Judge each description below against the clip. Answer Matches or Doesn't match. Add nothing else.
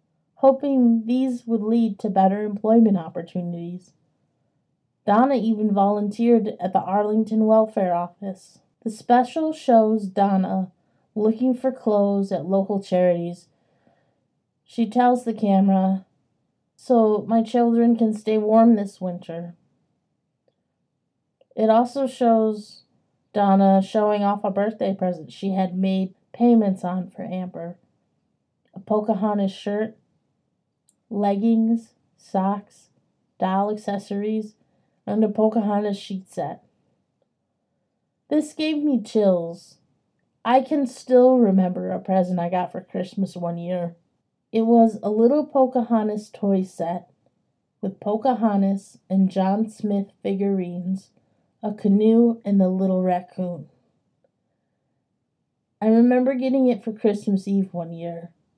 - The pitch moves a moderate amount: Matches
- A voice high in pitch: Matches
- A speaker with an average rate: Doesn't match